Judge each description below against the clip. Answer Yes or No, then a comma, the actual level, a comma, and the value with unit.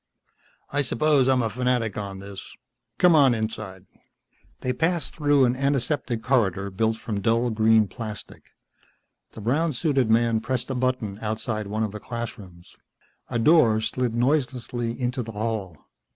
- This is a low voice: Yes, low, 115 Hz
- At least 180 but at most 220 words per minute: No, average, 150 wpm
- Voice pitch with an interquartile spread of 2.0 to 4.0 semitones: Yes, average, 3.1 semitones